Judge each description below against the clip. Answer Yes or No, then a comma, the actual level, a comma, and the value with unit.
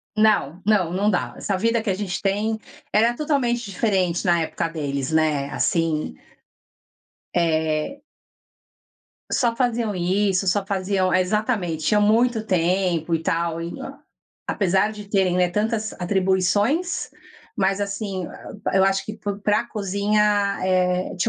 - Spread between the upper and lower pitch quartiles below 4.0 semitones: Yes, average, 3.3 semitones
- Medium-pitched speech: No, high, 195 Hz